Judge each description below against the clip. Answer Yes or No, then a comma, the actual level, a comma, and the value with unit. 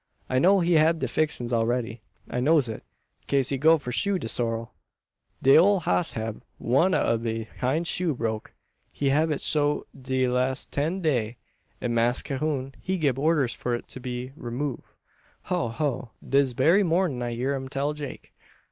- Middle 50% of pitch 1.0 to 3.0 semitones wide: No, average, 4.3 semitones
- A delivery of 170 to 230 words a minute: Yes, average, 180 wpm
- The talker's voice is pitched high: No, low, 135 Hz